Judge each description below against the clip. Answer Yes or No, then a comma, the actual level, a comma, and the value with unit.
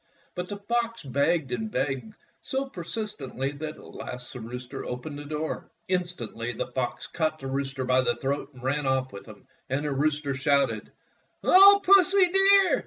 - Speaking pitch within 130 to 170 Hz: Yes, medium, 140 Hz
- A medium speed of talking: Yes, average, 180 wpm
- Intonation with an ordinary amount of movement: No, wide, 6.3 semitones